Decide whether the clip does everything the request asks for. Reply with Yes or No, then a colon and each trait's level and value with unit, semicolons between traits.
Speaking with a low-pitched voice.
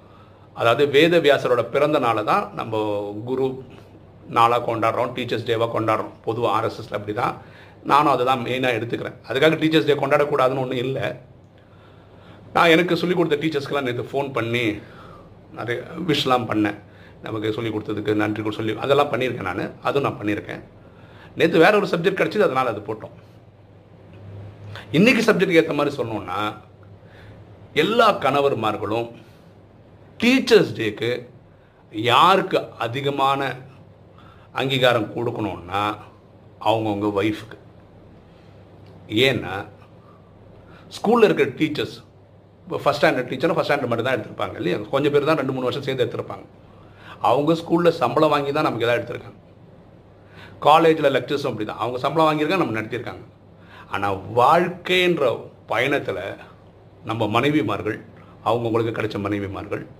Yes: low, 115 Hz